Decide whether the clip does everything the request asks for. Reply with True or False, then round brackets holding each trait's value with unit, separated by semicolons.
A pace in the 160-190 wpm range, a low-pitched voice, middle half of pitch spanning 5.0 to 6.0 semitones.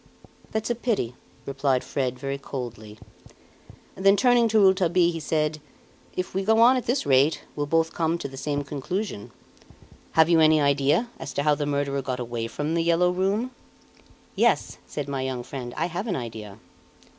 False (180 wpm; 150 Hz; 5.5 semitones)